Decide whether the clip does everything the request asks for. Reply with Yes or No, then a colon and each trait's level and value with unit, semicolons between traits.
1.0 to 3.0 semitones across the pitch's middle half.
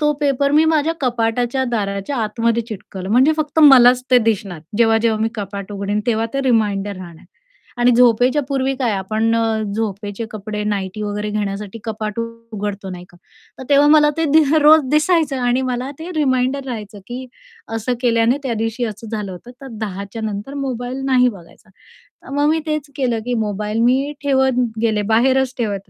No: average, 4.1 semitones